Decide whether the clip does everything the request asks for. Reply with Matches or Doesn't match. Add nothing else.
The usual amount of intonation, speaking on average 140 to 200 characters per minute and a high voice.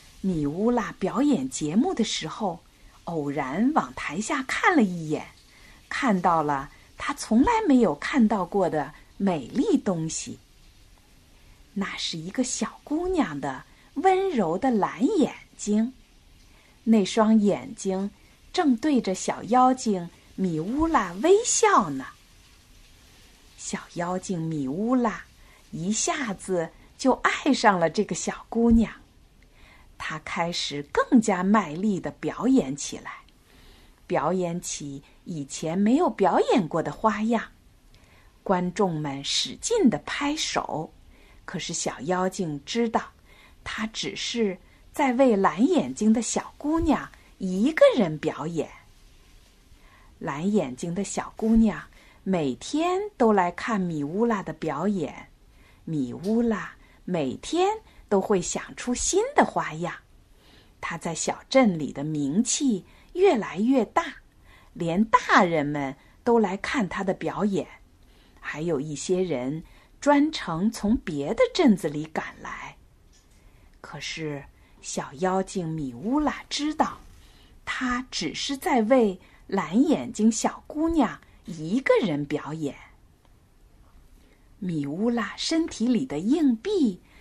Doesn't match